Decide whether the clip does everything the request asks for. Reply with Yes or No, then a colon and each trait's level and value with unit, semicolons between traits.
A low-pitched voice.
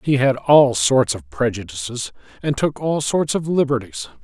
Yes: low, 125 Hz